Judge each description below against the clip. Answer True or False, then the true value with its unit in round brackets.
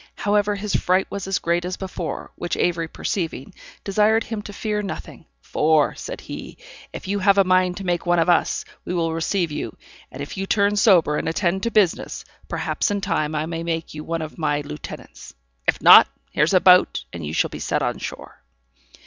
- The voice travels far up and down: False (3.5 semitones)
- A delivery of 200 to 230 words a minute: True (205 wpm)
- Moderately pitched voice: True (180 Hz)